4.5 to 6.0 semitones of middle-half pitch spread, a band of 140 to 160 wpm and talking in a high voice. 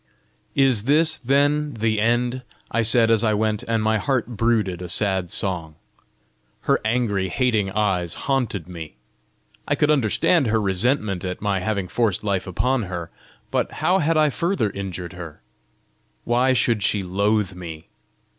No: average, 4.8 semitones; average, 155 wpm; low, 110 Hz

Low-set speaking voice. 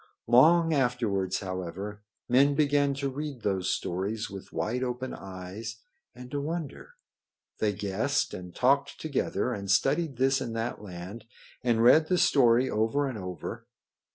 Yes: low, 120 Hz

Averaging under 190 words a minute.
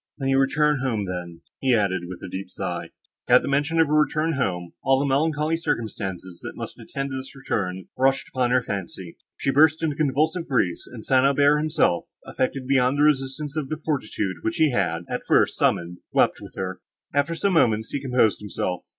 No: average, 195 wpm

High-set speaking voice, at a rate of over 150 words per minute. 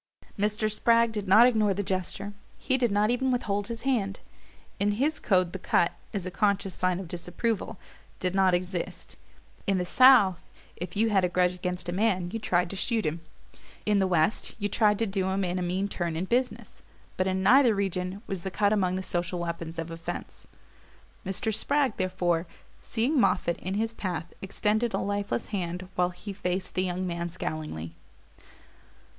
Yes: high, 195 Hz; average, 185 wpm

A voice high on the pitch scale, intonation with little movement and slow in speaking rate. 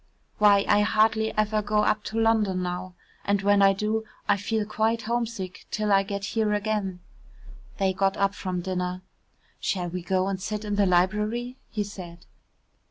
No: high, 205 Hz; narrow, 2.2 semitones; average, 170 wpm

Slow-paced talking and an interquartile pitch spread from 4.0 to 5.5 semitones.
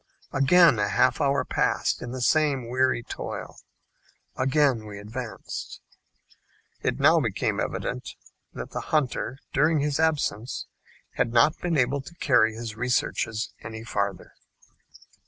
Yes: slow, 130 wpm; average, 4.4 semitones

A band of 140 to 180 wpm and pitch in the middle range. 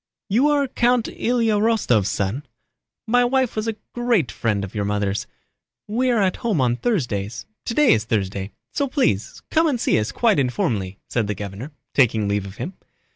Yes: average, 175 wpm; medium, 145 Hz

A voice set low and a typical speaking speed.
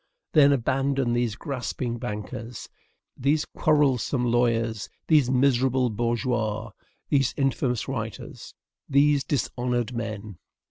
No: low, 125 Hz; slow, 95 wpm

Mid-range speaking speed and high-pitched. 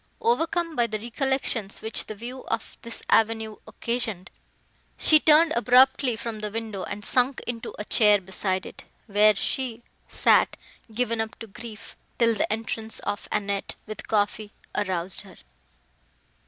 Yes: average, 145 wpm; high, 225 Hz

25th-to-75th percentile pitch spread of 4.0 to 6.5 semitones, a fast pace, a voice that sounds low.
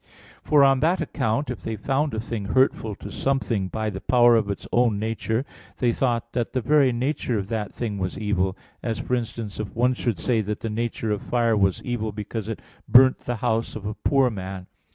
No: average, 3.0 semitones; fast, 215 wpm; low, 115 Hz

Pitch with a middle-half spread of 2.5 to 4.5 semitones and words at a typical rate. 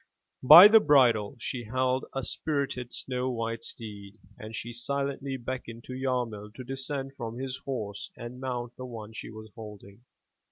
Yes: average, 2.9 semitones; average, 160 wpm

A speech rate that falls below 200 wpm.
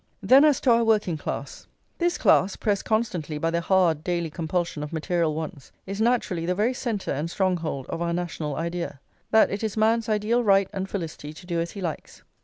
No: fast, 205 wpm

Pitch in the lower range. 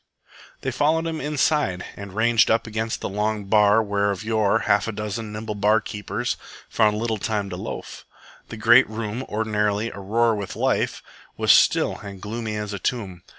Yes: low, 110 Hz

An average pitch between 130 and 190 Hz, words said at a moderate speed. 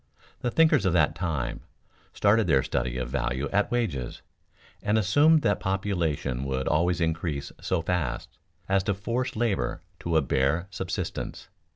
No: very low, 85 Hz; average, 150 wpm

